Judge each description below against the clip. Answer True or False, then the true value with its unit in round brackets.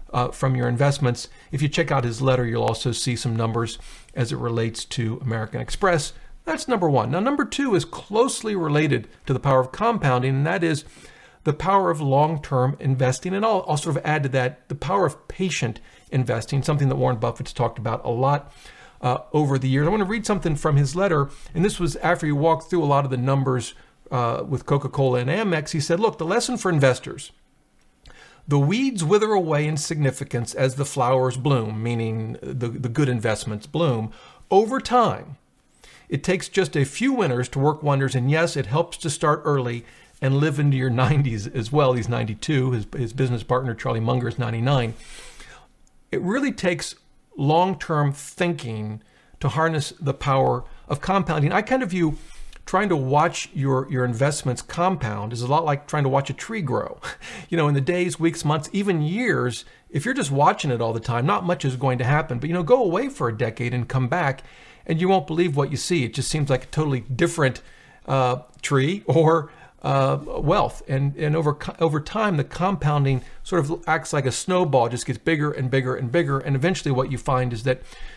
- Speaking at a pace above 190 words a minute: True (205 wpm)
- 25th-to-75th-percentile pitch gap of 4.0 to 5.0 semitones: True (4.6 semitones)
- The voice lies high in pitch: False (140 Hz)